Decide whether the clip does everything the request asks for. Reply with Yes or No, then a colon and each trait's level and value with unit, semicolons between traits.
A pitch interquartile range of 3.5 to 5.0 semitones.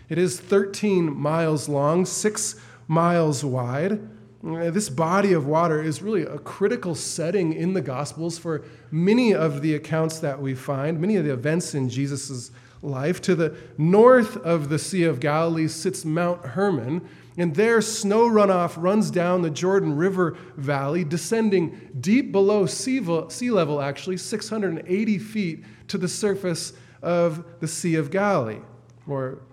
Yes: average, 4.3 semitones